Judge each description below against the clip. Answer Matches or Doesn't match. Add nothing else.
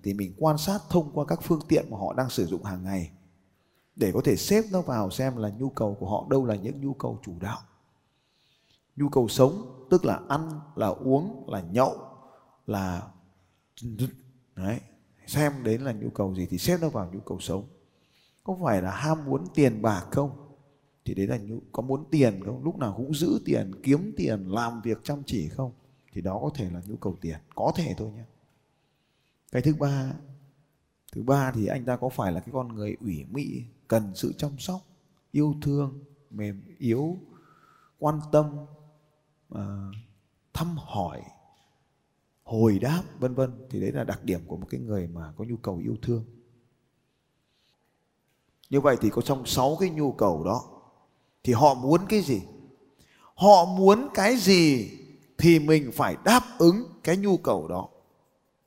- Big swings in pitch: Matches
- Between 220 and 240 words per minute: Doesn't match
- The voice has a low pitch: Matches